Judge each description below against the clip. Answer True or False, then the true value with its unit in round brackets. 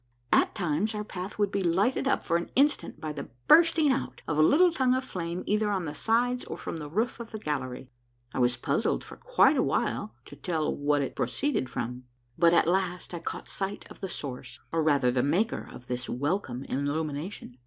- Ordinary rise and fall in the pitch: False (6.9 semitones)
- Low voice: False (170 Hz)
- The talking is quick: True (210 wpm)